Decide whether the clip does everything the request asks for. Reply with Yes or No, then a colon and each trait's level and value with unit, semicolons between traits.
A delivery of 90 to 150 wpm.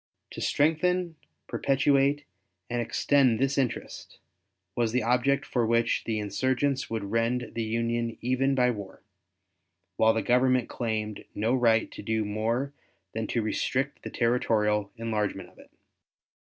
Yes: average, 140 wpm